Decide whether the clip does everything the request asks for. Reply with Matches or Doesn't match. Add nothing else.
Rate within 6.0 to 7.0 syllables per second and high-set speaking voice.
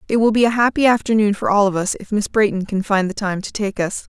Matches